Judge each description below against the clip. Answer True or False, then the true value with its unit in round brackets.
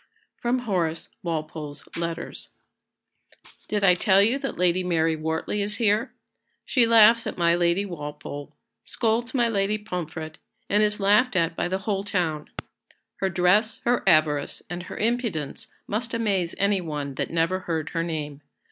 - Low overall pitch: False (185 Hz)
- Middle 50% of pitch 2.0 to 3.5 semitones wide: False (4.6 semitones)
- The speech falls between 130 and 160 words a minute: True (155 wpm)